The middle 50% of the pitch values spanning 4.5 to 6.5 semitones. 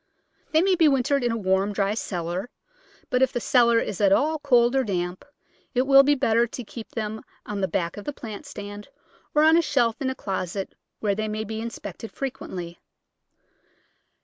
Yes: average, 4.9 semitones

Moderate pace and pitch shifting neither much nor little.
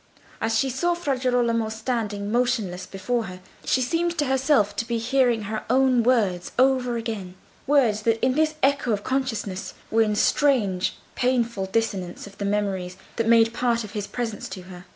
Yes: average, 175 wpm; average, 3.9 semitones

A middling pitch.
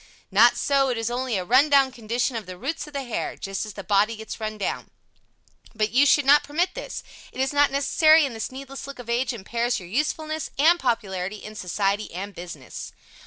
No: high, 240 Hz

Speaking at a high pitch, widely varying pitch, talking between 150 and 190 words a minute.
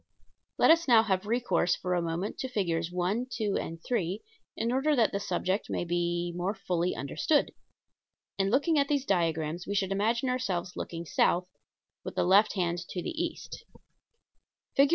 Yes: high, 195 Hz; wide, 5.7 semitones; average, 175 wpm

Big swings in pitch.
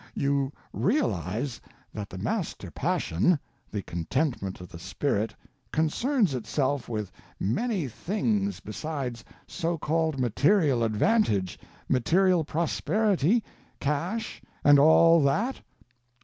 Yes: wide, 8.1 semitones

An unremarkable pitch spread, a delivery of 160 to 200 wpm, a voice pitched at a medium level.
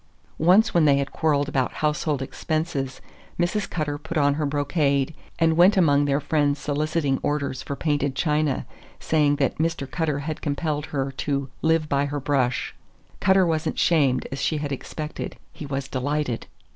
No: narrow, 2.2 semitones; average, 170 wpm; medium, 145 Hz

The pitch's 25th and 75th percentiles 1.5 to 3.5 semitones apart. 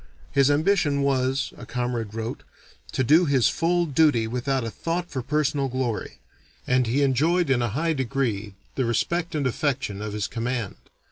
No: average, 4.0 semitones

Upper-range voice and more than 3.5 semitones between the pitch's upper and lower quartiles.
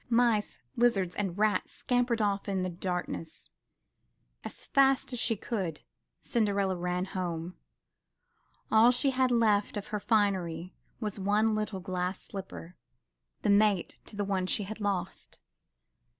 No: high, 200 Hz; average, 3.2 semitones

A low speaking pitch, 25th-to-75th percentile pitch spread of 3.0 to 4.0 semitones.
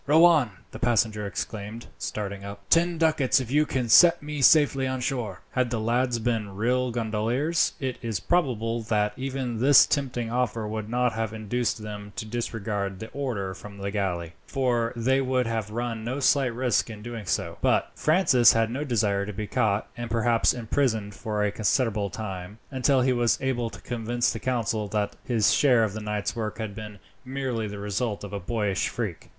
Yes: low, 115 Hz; average, 3.4 semitones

